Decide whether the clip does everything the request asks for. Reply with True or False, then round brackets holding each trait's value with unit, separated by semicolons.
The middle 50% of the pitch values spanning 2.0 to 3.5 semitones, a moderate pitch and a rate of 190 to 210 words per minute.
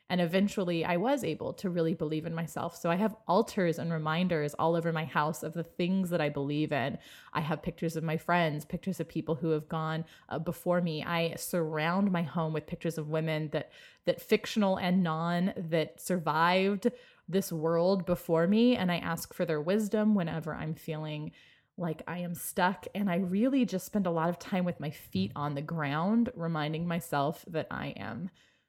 True (2.4 semitones; 170 Hz; 195 wpm)